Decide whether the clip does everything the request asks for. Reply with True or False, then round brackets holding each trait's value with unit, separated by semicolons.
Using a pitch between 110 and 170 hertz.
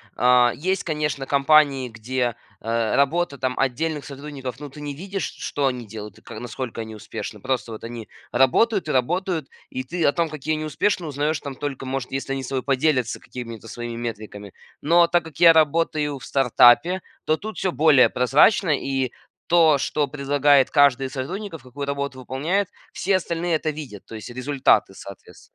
True (140 Hz)